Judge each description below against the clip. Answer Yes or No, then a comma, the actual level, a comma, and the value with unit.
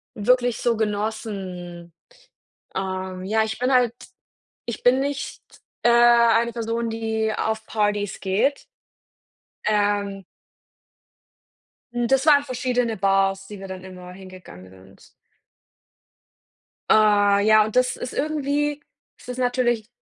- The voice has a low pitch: No, high, 220 Hz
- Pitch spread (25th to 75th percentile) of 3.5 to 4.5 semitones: Yes, average, 3.9 semitones